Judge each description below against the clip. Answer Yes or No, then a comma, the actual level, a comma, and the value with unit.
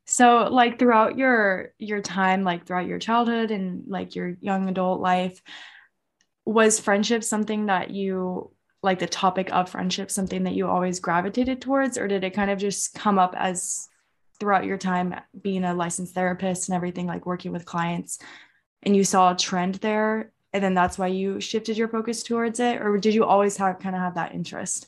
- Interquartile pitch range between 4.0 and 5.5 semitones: No, average, 3.2 semitones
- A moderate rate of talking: Yes, average, 195 wpm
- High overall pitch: Yes, high, 195 Hz